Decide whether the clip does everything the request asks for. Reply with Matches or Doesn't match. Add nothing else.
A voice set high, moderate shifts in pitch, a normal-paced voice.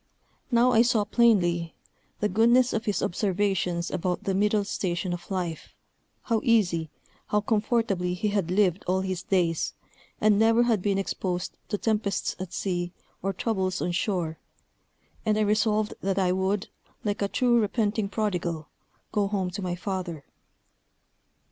Matches